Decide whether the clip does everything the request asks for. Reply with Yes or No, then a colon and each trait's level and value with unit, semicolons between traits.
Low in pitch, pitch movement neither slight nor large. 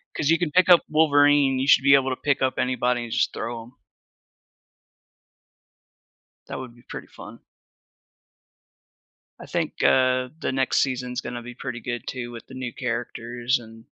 No: low, 125 Hz; narrow, 2.2 semitones